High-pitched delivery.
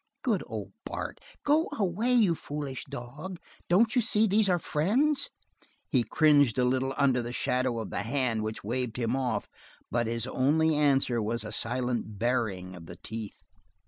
No: low, 130 Hz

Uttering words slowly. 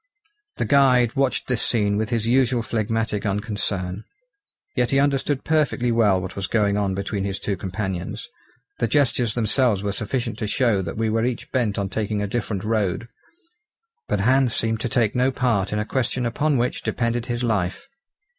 No: average, 180 wpm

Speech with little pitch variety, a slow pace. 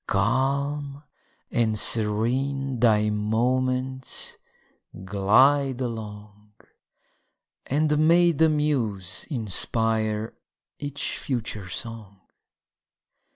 No: average, 4.5 semitones; slow, 65 wpm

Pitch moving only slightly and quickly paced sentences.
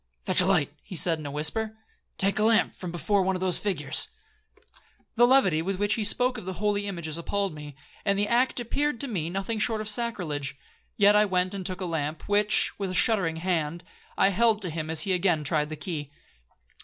No: average, 4.5 semitones; fast, 215 wpm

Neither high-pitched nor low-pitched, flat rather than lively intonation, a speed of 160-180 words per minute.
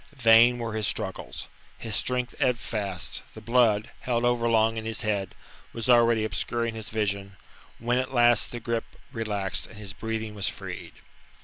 No: low, 115 Hz; narrow, 2.0 semitones; average, 165 wpm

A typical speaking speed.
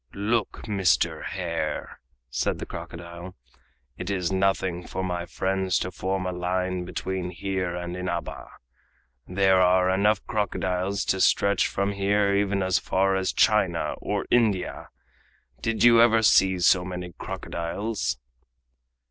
No: slow, 130 wpm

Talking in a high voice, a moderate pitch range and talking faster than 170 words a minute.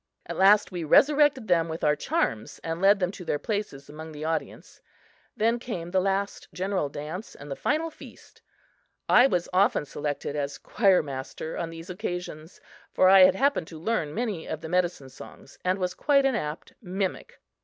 No: medium, 180 Hz; average, 4.7 semitones; average, 185 wpm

